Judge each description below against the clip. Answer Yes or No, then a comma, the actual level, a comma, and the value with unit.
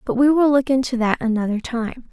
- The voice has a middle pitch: No, very high, 250 Hz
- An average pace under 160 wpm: No, fast, 225 wpm